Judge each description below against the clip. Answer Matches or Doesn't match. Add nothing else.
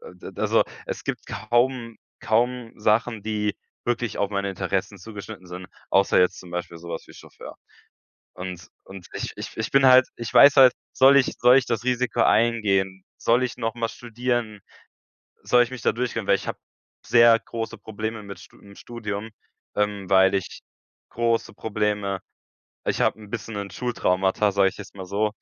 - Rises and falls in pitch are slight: Doesn't match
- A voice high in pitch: Doesn't match